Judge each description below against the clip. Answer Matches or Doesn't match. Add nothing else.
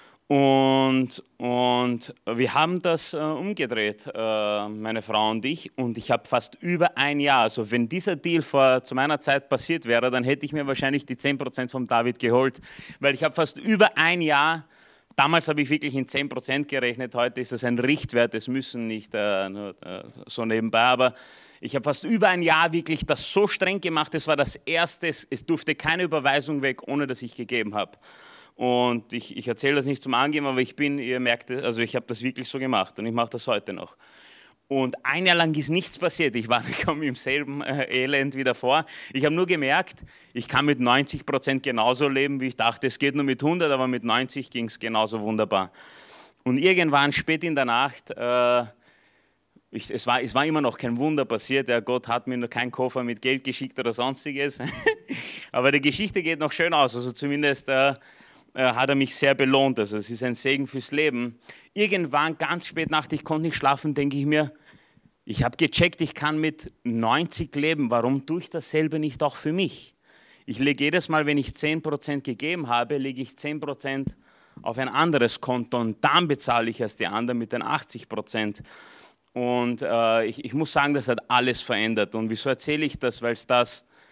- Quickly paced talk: Matches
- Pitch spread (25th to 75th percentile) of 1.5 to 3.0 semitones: Doesn't match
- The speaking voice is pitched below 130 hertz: Doesn't match